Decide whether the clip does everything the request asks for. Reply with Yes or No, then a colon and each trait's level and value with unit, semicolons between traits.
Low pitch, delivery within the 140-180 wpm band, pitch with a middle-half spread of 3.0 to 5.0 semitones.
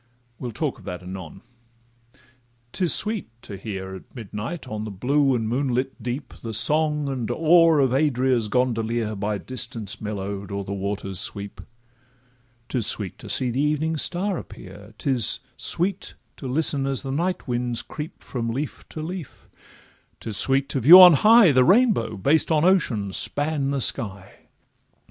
No: low, 125 Hz; average, 155 wpm; wide, 5.6 semitones